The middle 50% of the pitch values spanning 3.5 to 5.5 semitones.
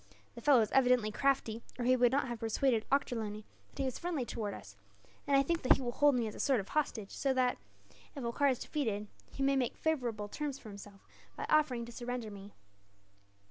Yes: average, 3.9 semitones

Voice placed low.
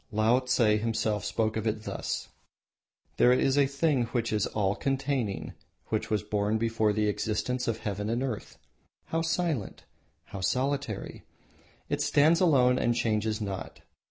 Yes: low, 115 Hz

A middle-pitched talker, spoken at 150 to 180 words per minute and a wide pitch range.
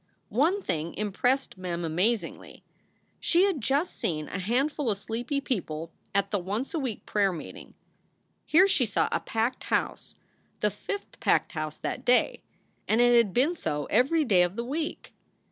No: high, 230 Hz; average, 170 wpm; wide, 6.9 semitones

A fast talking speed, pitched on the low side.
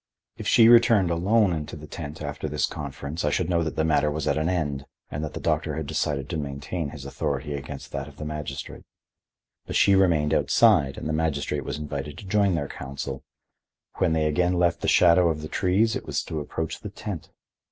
Yes: fast, 215 wpm; very low, 75 Hz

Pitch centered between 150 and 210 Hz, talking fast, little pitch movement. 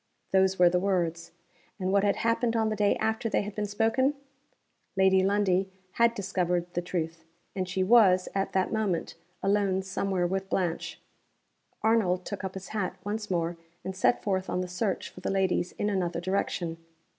No: high, 190 Hz; average, 180 wpm; narrow, 2.3 semitones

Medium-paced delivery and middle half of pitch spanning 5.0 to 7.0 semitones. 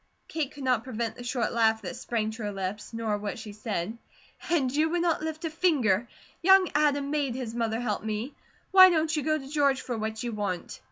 No: fast, 220 wpm; wide, 5.6 semitones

